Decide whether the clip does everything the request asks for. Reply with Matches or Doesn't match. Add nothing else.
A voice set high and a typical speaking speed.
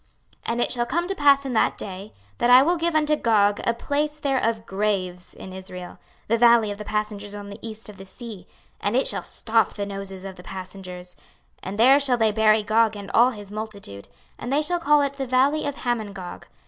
Doesn't match